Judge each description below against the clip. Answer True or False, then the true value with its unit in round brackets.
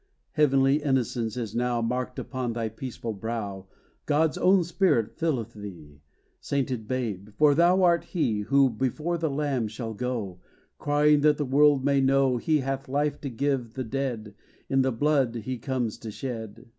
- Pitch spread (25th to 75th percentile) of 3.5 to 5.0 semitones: True (4.1 semitones)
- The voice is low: True (130 Hz)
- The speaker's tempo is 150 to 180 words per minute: True (165 wpm)